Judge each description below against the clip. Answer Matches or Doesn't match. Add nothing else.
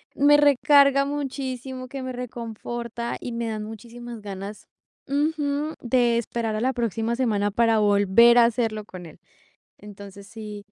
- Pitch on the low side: Doesn't match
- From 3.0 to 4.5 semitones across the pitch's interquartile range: Matches